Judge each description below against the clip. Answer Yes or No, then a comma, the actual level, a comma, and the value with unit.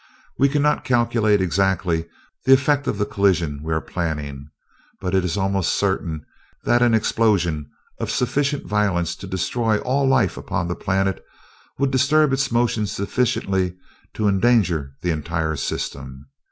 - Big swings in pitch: Yes, wide, 6.2 semitones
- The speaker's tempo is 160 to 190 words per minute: No, average, 145 wpm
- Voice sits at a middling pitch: No, very low, 95 Hz